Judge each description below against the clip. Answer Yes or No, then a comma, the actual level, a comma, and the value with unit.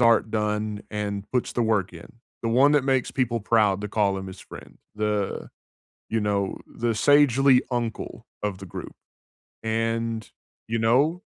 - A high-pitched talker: No, low, 110 Hz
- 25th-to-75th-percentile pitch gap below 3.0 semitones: Yes, narrow, 2.5 semitones